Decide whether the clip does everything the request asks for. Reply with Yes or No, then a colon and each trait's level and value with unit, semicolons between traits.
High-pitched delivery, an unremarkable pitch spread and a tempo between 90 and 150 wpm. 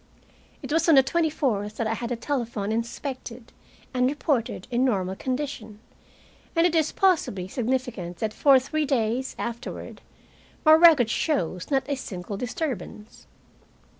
Yes: very high, 250 Hz; average, 5.0 semitones; average, 145 wpm